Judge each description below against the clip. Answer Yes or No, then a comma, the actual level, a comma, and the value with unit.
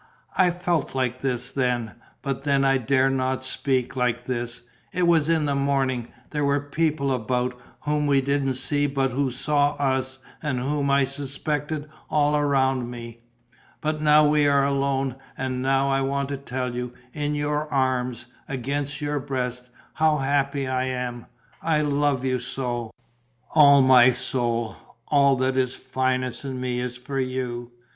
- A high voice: No, low, 135 Hz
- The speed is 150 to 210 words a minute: Yes, average, 160 wpm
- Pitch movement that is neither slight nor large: No, narrow, 2.1 semitones